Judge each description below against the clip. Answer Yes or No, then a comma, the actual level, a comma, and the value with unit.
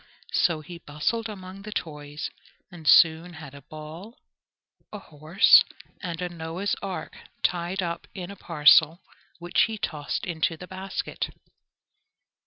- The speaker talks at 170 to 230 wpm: No, slow, 135 wpm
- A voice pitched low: No, medium, 170 Hz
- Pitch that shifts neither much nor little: Yes, average, 3.3 semitones